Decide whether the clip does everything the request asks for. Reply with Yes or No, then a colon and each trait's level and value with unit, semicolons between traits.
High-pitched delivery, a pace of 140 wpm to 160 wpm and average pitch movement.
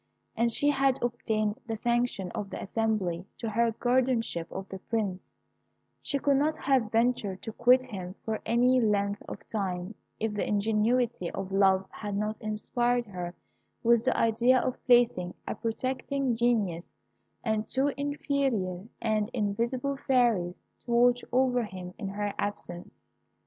Yes: high, 225 Hz; average, 150 wpm; average, 3.6 semitones